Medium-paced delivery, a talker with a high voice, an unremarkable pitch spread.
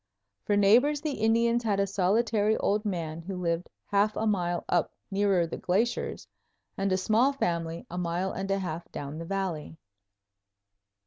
Yes: average, 165 wpm; high, 195 Hz; average, 3.7 semitones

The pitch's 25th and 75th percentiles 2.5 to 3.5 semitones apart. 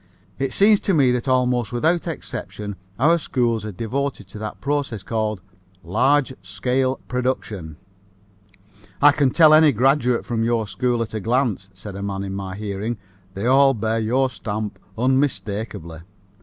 No: average, 4.3 semitones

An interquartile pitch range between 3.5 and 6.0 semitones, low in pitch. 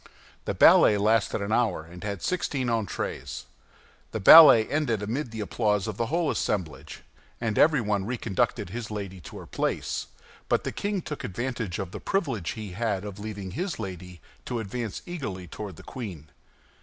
Yes: average, 4.2 semitones; low, 110 Hz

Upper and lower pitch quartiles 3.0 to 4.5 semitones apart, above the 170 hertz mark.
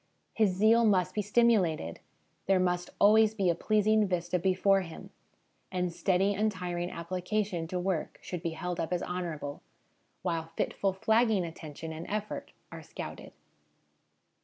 Yes: average, 3.3 semitones; medium, 185 Hz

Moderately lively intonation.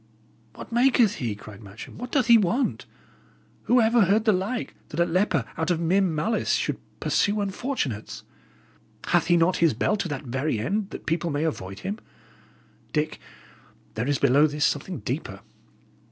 No: wide, 6.6 semitones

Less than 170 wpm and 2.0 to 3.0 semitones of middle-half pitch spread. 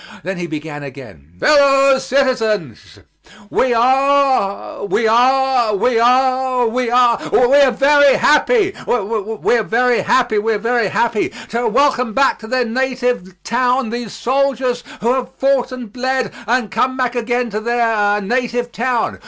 Yes: average, 150 wpm; average, 2.7 semitones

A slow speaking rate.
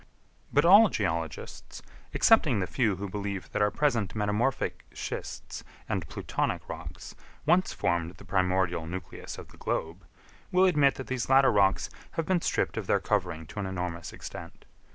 No: average, 160 wpm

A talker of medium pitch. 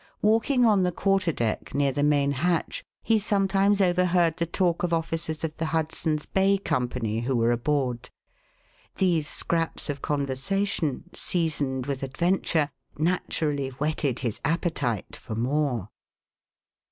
Yes: medium, 155 Hz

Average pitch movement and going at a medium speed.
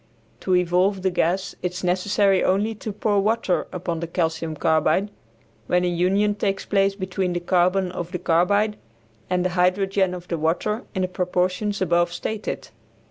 No: narrow, 1.9 semitones; average, 170 wpm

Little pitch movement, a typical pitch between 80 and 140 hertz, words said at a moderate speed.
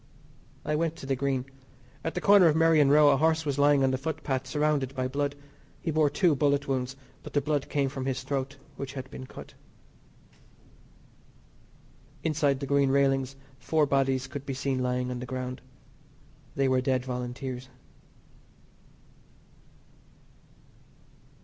Yes: narrow, 2.0 semitones; low, 135 Hz; average, 150 wpm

